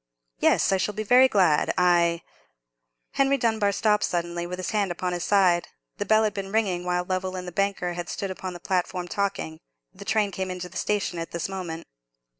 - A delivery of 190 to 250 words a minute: Yes, fast, 205 wpm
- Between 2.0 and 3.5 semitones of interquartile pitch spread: Yes, narrow, 2.5 semitones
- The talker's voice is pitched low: No, medium, 185 Hz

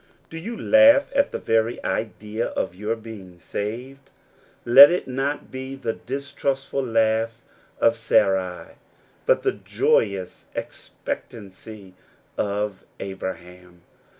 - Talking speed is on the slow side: Yes, slow, 110 wpm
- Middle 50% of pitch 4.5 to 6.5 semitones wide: Yes, average, 5.3 semitones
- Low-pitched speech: Yes, low, 115 Hz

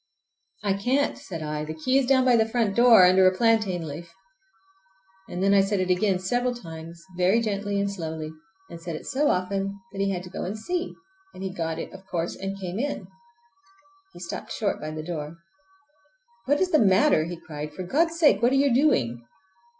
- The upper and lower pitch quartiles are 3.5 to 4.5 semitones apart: No, wide, 5.6 semitones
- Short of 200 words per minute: No, fast, 205 wpm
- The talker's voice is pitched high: Yes, high, 195 Hz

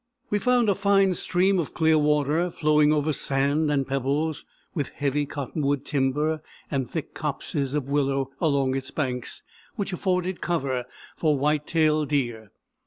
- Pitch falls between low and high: Yes, medium, 150 Hz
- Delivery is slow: No, average, 150 wpm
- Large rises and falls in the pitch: No, average, 2.8 semitones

